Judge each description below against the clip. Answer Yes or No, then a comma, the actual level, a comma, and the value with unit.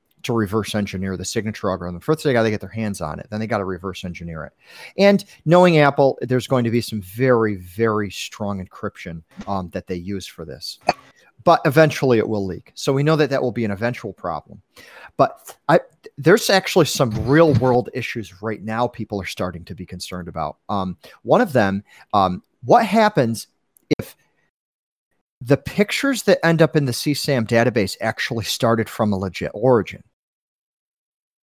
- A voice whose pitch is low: Yes, low, 115 Hz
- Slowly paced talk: No, average, 180 wpm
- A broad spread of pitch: Yes, wide, 6.3 semitones